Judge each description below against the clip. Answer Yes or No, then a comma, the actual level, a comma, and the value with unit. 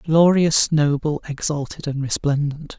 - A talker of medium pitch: Yes, medium, 150 Hz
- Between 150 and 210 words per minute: No, slow, 110 wpm